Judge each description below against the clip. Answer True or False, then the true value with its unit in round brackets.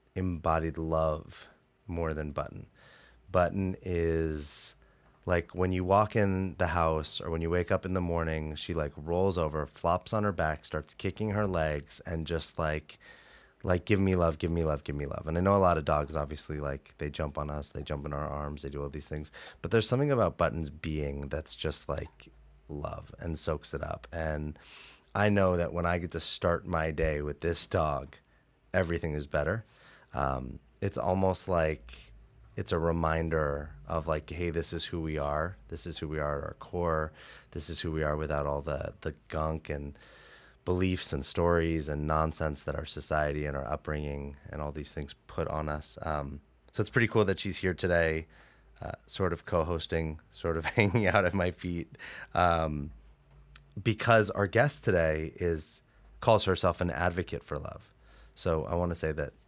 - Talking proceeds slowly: False (195 wpm)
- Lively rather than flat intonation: False (3.2 semitones)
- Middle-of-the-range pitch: False (80 Hz)